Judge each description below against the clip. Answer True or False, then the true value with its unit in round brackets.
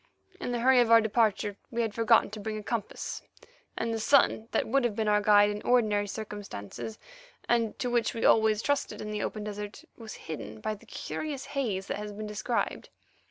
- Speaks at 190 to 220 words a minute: True (205 wpm)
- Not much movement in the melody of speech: True (2.2 semitones)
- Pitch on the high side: True (215 Hz)